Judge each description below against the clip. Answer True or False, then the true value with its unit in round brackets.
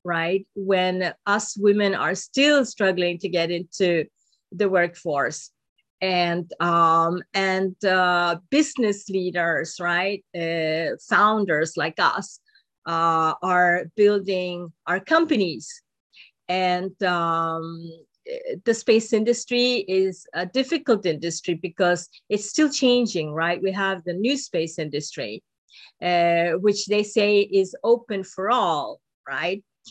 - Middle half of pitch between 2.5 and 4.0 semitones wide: True (3.3 semitones)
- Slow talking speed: True (115 wpm)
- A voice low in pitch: False (185 Hz)